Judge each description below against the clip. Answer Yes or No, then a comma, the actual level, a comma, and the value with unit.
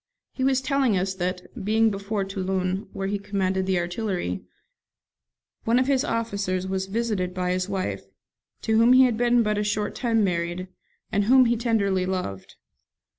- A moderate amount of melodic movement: Yes, average, 3.6 semitones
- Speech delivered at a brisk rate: No, average, 170 wpm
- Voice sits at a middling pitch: No, high, 200 Hz